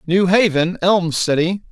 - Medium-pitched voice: Yes, medium, 180 Hz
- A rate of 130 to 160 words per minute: Yes, average, 140 wpm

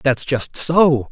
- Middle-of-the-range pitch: Yes, medium, 145 Hz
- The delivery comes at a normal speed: Yes, average, 160 wpm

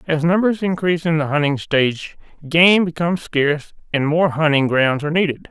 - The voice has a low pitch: No, medium, 160 Hz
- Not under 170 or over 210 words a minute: Yes, average, 175 wpm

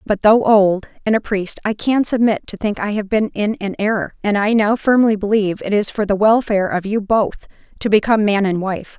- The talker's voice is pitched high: Yes, high, 210 Hz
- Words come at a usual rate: No, fast, 235 wpm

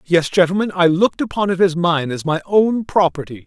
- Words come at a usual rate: No, fast, 210 wpm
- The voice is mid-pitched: Yes, medium, 175 Hz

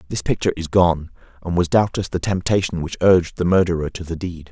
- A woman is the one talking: No, male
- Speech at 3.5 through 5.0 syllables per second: No, 6.1 syllables/s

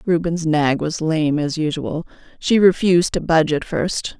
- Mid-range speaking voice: Yes, medium, 160 Hz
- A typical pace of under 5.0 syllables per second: Yes, 4.6 syllables/s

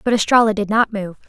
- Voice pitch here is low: No, high, 210 Hz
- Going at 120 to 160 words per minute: No, fast, 235 wpm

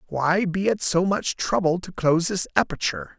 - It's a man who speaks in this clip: Yes, male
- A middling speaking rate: Yes, average, 190 wpm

